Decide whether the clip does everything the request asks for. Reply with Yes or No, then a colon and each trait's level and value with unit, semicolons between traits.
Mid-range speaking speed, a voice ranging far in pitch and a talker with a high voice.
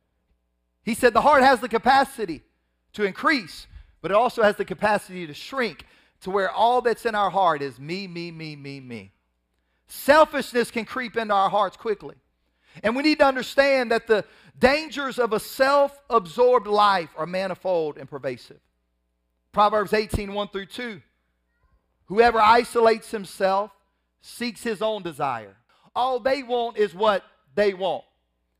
Yes: average, 150 wpm; wide, 7.0 semitones; high, 210 Hz